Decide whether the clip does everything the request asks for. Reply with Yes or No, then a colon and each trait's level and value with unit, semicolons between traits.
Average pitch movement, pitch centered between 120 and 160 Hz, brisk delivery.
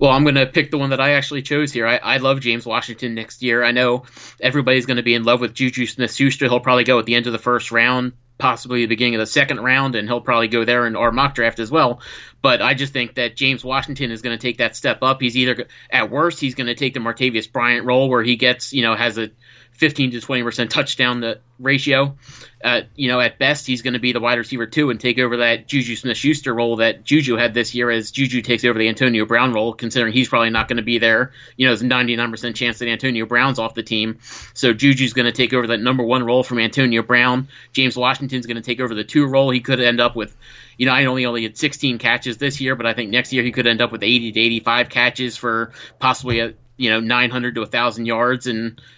No: narrow, 1.7 semitones; low, 125 Hz; fast, 260 wpm